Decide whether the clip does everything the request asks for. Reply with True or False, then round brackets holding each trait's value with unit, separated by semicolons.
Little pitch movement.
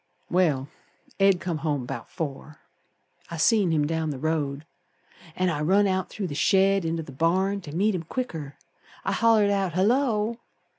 False (4.4 semitones)